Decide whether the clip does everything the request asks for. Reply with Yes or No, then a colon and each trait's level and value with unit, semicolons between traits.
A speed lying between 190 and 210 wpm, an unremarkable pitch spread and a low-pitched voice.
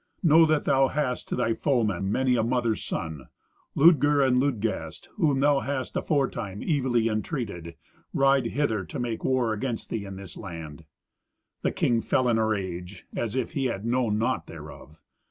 No: average, 170 wpm; average, 4.8 semitones; low, 120 Hz